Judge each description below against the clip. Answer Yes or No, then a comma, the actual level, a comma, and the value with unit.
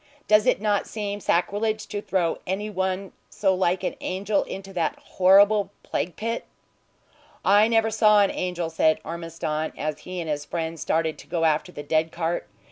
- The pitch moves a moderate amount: Yes, average, 3.8 semitones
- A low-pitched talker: No, medium, 185 Hz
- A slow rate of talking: No, average, 175 wpm